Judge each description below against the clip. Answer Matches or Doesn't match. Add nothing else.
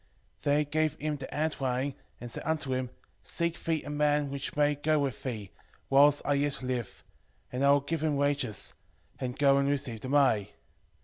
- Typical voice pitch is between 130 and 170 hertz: Matches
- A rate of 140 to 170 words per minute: Doesn't match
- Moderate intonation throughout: Doesn't match